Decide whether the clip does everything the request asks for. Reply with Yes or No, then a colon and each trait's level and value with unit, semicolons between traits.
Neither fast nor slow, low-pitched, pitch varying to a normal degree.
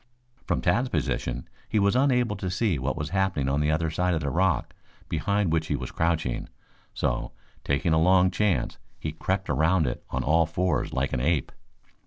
Yes: average, 190 wpm; very low, 85 Hz; average, 3.9 semitones